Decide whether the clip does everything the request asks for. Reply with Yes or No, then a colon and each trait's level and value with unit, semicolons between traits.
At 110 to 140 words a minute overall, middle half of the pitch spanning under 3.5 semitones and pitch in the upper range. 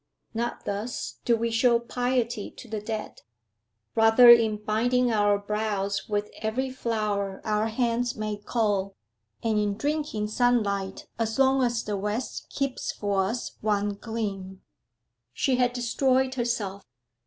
Yes: slow, 135 wpm; average, 2.8 semitones; high, 220 Hz